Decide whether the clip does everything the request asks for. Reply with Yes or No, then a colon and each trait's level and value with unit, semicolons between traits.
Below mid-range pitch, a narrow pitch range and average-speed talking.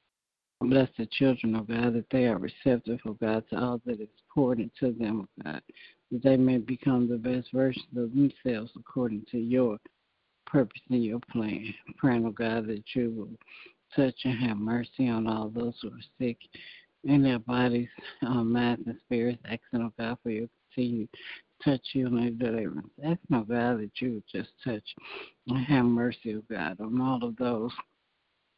Yes: low, 120 Hz; narrow, 1.9 semitones; average, 195 wpm